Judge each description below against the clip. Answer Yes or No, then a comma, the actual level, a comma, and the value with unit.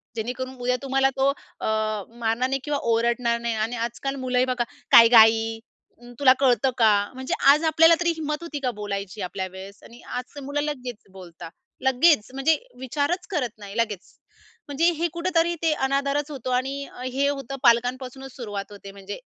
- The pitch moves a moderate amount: Yes, average, 3.7 semitones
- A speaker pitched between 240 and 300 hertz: Yes, very high, 255 Hz